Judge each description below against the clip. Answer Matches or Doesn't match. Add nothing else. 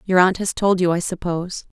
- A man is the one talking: Doesn't match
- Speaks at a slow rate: Doesn't match